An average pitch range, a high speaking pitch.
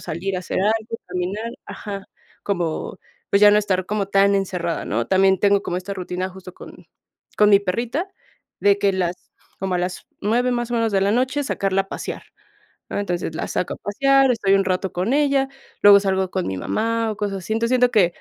Yes: average, 3.3 semitones; high, 200 Hz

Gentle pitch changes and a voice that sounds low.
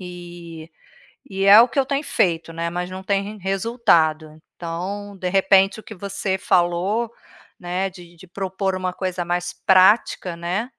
No: narrow, 2.3 semitones; medium, 185 Hz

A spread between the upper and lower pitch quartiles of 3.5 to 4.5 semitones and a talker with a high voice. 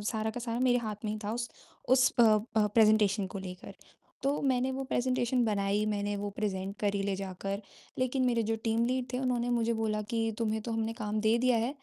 No: average, 2.7 semitones; high, 225 Hz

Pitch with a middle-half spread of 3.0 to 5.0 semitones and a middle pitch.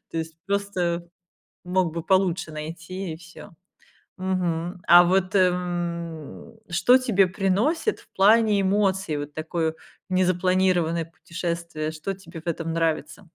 No: narrow, 2.4 semitones; medium, 175 Hz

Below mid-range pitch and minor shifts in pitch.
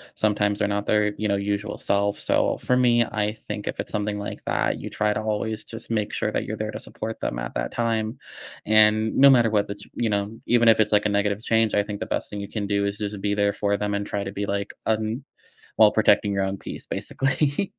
Yes: low, 105 Hz; narrow, 1.5 semitones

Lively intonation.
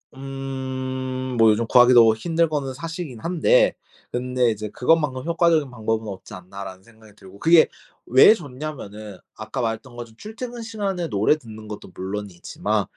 Yes: wide, 6.0 semitones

